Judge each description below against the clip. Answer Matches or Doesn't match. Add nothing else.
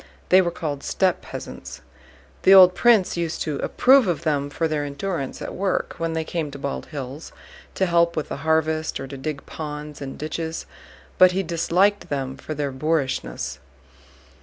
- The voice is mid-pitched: Matches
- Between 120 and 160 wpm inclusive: Doesn't match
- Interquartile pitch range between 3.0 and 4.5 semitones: Matches